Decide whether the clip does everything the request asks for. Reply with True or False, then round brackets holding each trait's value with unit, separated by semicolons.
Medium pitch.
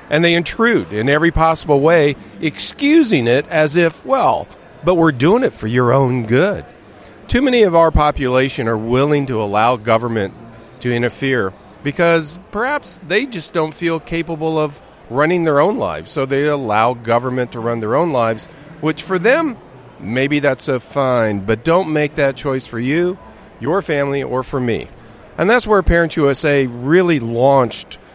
True (145 Hz)